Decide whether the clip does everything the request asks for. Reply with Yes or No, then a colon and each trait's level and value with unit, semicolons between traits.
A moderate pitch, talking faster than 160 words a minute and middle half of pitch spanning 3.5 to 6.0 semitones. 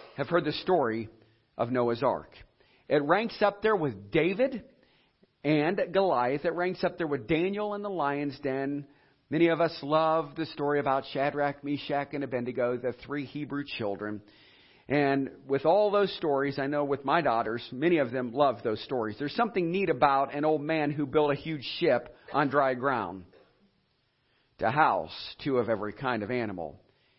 Yes: medium, 145 Hz; average, 175 wpm; average, 4.0 semitones